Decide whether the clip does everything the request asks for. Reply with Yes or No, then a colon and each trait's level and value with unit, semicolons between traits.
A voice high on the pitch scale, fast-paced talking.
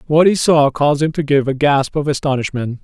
No: medium, 145 Hz; fast, 235 wpm